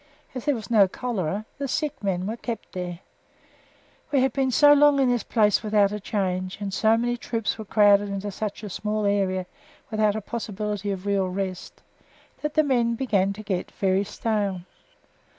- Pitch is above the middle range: Yes, high, 210 Hz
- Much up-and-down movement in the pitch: No, average, 3.2 semitones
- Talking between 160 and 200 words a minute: Yes, average, 185 wpm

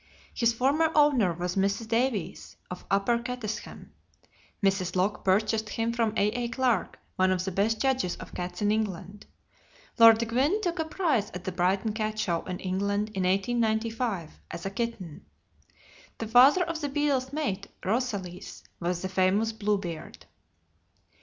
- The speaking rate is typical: Yes, average, 150 wpm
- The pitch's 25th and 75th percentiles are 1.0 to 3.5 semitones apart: No, average, 4.3 semitones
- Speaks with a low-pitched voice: No, high, 215 Hz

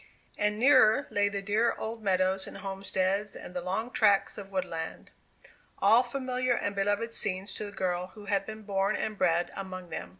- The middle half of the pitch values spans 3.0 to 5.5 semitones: No, narrow, 2.5 semitones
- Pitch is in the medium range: No, high, 200 Hz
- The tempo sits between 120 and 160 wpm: No, average, 180 wpm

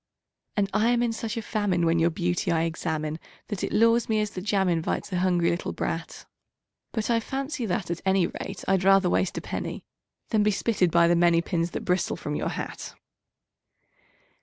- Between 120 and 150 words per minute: No, average, 200 wpm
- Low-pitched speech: No, medium, 185 Hz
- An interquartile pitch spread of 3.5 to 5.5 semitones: Yes, average, 3.9 semitones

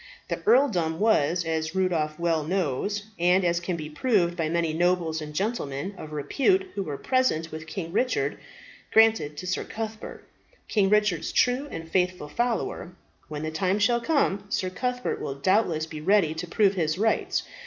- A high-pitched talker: No, medium, 180 Hz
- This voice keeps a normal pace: Yes, average, 170 wpm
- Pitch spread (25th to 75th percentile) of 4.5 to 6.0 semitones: Yes, average, 4.9 semitones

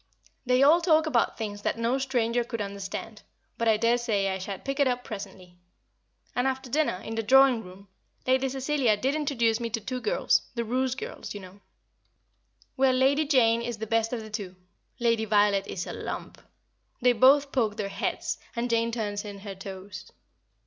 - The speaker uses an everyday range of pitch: Yes, average, 4.1 semitones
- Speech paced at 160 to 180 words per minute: No, average, 190 wpm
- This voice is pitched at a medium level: No, high, 230 Hz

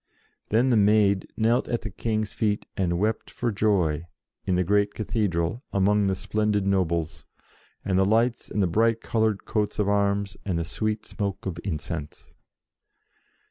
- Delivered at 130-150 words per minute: No, average, 160 wpm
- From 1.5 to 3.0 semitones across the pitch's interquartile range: Yes, narrow, 2.5 semitones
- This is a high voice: No, low, 100 Hz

